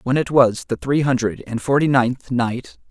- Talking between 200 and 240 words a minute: Yes, fast, 205 wpm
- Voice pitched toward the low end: Yes, low, 130 Hz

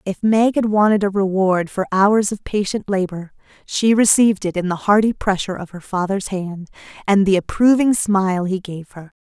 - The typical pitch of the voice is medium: No, high, 195 Hz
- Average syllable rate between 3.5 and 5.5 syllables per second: Yes, 5.1 syllables/s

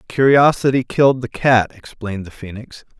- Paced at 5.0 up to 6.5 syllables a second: Yes, 5.2 syllables/s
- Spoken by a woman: No, male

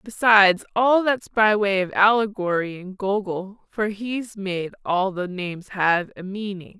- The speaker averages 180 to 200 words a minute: No, average, 160 wpm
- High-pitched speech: Yes, high, 200 Hz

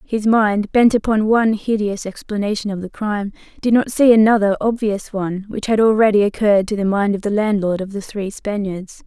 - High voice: Yes, high, 210 Hz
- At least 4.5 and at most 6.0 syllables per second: Yes, 5.5 syllables/s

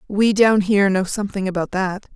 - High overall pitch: Yes, high, 195 Hz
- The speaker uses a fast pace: No, average, 195 wpm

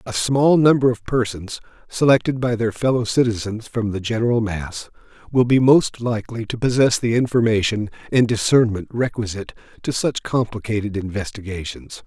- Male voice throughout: Yes, male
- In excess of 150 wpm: No, average, 145 wpm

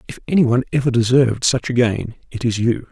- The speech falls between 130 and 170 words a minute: No, fast, 205 wpm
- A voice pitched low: Yes, low, 120 Hz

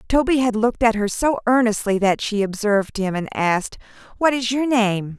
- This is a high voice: Yes, high, 225 Hz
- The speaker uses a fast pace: No, average, 195 wpm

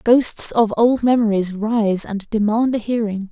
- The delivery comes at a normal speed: Yes, average, 165 wpm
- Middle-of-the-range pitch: No, high, 220 Hz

